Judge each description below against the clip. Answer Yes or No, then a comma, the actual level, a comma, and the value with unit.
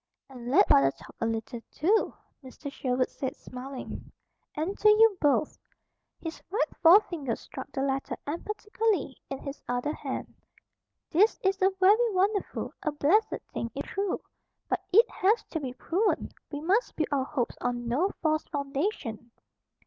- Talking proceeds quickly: No, average, 155 wpm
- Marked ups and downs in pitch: Yes, wide, 7.0 semitones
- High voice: Yes, very high, 305 Hz